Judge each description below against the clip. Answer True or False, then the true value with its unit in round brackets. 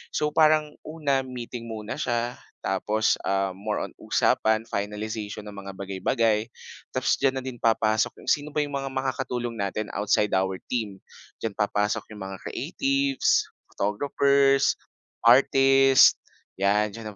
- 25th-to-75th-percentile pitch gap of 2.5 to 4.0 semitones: False (4.5 semitones)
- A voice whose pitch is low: True (115 Hz)